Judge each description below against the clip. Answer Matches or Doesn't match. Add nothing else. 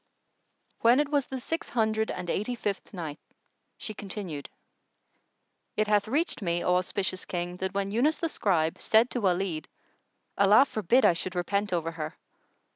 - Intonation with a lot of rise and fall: Doesn't match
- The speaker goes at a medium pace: Matches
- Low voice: Doesn't match